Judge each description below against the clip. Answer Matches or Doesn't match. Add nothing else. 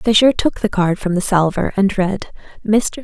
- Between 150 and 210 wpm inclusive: Matches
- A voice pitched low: Doesn't match